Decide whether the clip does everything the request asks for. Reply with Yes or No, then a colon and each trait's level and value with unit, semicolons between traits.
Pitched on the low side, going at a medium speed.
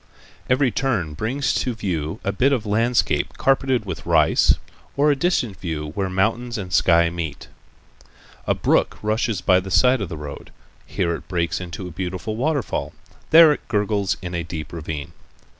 Yes: low, 100 Hz; average, 170 wpm